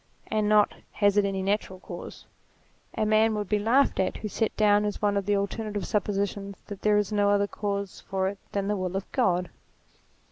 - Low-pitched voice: No, high, 205 Hz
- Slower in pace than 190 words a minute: No, fast, 205 wpm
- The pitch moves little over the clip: Yes, narrow, 1.1 semitones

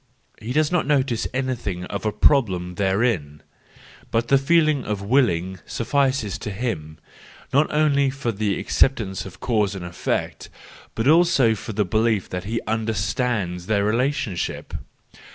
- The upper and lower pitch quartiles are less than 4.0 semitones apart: No, wide, 5.5 semitones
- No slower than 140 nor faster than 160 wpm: Yes, average, 145 wpm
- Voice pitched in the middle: No, low, 110 Hz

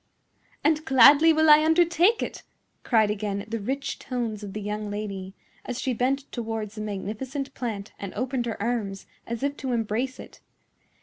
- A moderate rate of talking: Yes, average, 170 wpm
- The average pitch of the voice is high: Yes, high, 235 Hz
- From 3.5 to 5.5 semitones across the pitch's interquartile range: Yes, average, 4.5 semitones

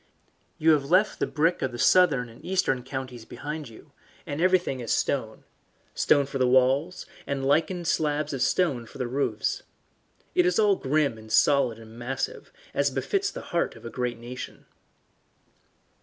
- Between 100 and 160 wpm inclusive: No, average, 170 wpm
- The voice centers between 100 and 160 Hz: Yes, medium, 140 Hz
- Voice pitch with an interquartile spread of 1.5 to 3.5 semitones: No, average, 5.0 semitones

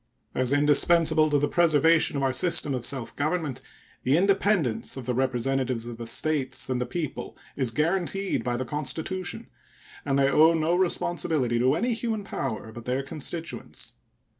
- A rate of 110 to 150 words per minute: No, average, 165 wpm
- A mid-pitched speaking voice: Yes, medium, 145 Hz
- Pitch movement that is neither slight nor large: Yes, average, 4.6 semitones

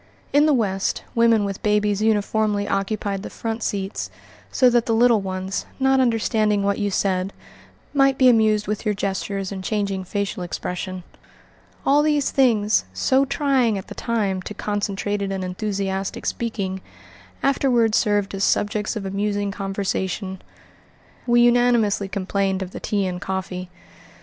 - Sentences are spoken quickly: No, average, 150 wpm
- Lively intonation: No, average, 2.8 semitones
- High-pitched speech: Yes, high, 205 Hz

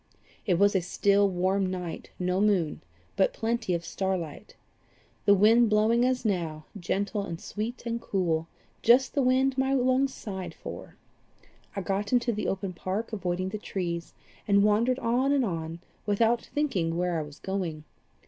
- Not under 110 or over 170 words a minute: Yes, average, 165 wpm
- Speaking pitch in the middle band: No, high, 200 Hz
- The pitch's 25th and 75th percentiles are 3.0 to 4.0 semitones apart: No, average, 4.7 semitones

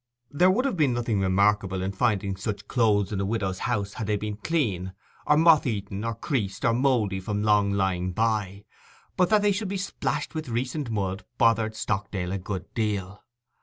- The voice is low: Yes, low, 105 Hz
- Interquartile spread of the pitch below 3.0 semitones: No, average, 3.9 semitones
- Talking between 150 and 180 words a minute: No, average, 190 wpm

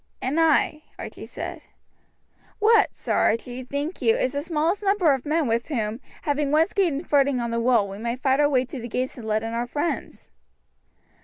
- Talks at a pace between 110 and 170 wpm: No, average, 200 wpm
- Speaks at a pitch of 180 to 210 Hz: No, very high, 275 Hz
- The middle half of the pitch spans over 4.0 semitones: Yes, average, 4.6 semitones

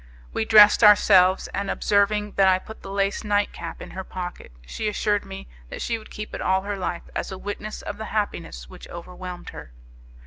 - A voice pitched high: Yes, high, 200 Hz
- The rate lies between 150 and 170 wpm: No, fast, 205 wpm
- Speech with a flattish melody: Yes, narrow, 2.1 semitones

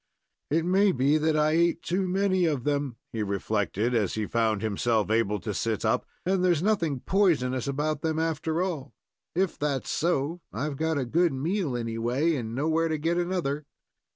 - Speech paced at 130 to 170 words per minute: No, average, 180 wpm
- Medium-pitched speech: Yes, medium, 150 Hz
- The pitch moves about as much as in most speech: No, wide, 5.9 semitones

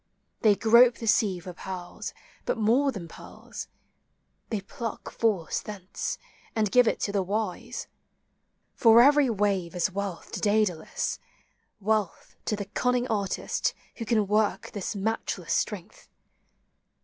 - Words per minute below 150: Yes, slow, 135 wpm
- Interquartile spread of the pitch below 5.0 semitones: Yes, average, 3.0 semitones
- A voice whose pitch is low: No, high, 210 Hz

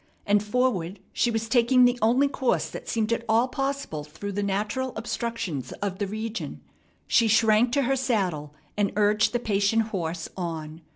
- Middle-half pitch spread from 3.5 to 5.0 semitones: Yes, average, 3.9 semitones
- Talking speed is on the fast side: No, average, 170 wpm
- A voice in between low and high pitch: No, high, 215 Hz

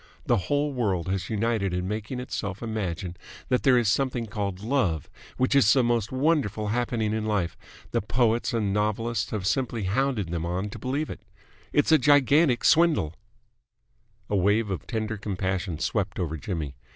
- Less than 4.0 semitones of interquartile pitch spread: No, average, 4.7 semitones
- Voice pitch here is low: Yes, low, 110 Hz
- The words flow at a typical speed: Yes, average, 165 wpm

